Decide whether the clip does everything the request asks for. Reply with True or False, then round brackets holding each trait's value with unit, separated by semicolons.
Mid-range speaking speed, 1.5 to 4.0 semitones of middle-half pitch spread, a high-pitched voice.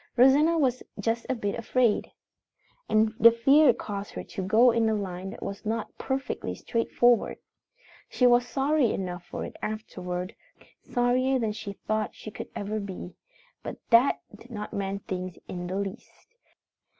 True (160 wpm; 3.7 semitones; 220 Hz)